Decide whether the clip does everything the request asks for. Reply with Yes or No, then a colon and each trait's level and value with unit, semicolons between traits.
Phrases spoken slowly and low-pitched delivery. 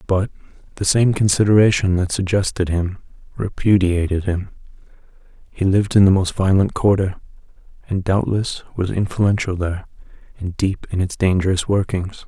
Yes: slow, 130 wpm; very low, 95 Hz